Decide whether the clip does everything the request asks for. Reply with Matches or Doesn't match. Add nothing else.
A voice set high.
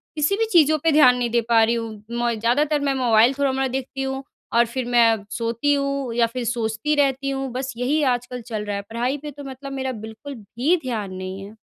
Matches